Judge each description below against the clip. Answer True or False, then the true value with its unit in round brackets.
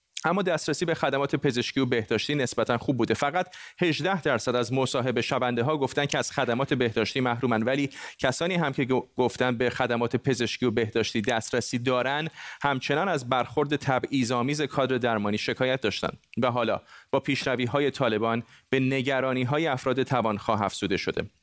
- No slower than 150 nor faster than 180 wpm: True (155 wpm)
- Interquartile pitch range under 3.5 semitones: True (2.8 semitones)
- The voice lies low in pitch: True (130 Hz)